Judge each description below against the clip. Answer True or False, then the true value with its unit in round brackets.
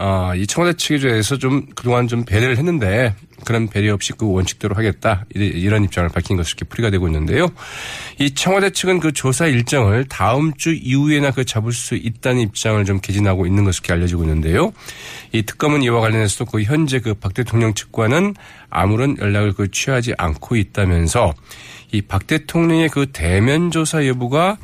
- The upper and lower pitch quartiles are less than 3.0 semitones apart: False (5.7 semitones)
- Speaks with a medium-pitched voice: False (115 Hz)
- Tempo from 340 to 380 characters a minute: True (375 characters per minute)